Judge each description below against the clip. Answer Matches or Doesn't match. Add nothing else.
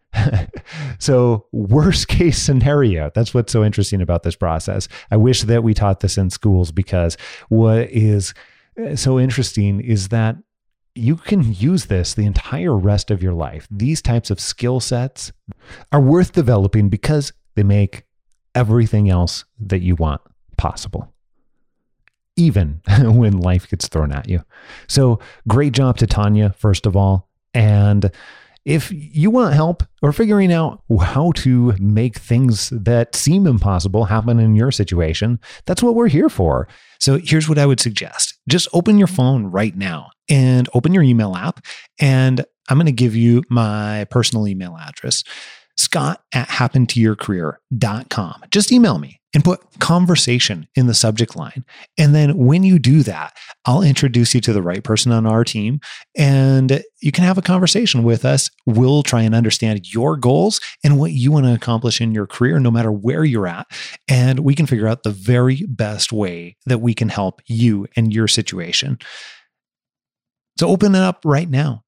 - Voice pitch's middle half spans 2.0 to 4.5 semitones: Doesn't match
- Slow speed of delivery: Doesn't match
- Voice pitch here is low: Matches